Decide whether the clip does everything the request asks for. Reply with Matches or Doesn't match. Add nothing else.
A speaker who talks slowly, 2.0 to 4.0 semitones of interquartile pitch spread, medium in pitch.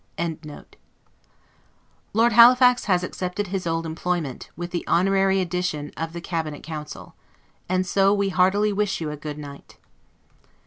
Doesn't match